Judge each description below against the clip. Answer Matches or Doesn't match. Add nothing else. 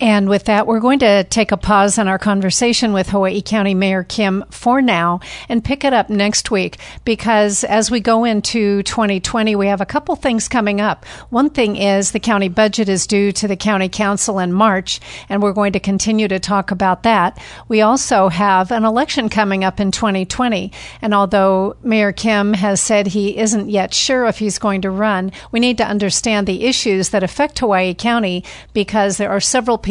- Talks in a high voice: Matches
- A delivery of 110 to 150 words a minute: Doesn't match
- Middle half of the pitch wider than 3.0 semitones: Doesn't match